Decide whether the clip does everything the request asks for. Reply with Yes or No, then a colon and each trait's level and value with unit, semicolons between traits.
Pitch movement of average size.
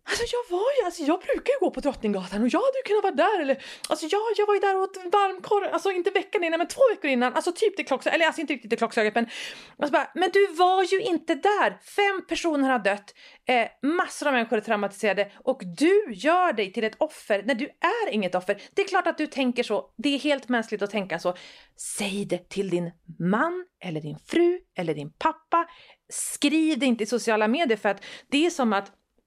No: wide, 8.8 semitones